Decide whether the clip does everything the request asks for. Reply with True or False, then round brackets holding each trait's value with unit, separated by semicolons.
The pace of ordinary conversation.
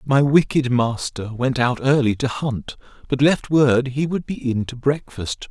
True (185 wpm)